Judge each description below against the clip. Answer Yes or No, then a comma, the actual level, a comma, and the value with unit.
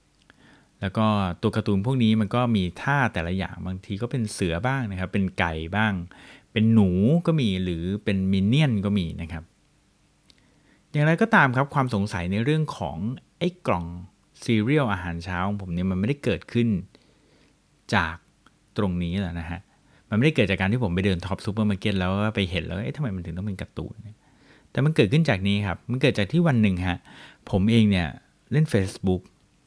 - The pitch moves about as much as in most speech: Yes, average, 4.6 semitones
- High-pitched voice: No, low, 100 Hz